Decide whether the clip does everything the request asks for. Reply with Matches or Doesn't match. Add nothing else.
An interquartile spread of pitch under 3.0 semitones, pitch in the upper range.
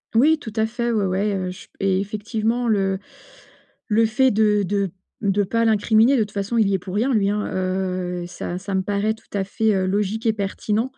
Matches